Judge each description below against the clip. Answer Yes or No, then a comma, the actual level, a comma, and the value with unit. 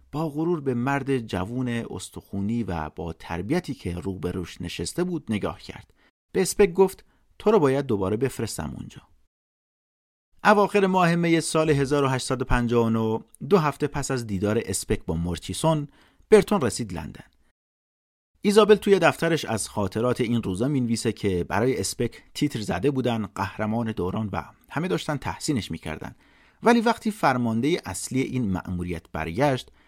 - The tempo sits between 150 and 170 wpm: No, average, 140 wpm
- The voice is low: Yes, low, 120 Hz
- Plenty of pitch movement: Yes, wide, 8.2 semitones